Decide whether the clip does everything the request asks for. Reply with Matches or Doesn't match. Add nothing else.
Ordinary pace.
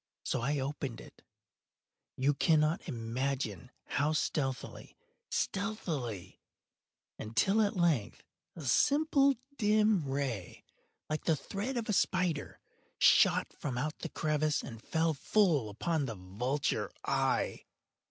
Doesn't match